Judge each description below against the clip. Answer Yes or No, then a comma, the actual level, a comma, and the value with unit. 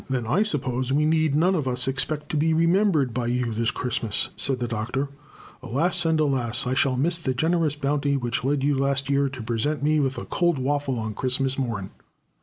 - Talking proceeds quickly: Yes, fast, 210 wpm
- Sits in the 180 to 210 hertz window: No, low, 135 Hz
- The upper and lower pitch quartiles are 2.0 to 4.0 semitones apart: Yes, average, 3.4 semitones